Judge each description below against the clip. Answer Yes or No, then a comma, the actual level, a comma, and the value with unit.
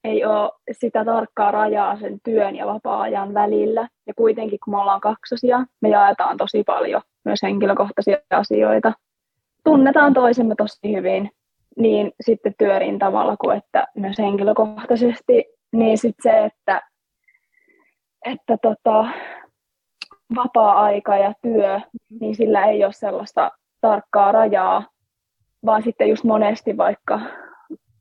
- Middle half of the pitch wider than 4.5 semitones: No, average, 2.7 semitones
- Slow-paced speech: No, average, 120 wpm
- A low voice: No, high, 220 Hz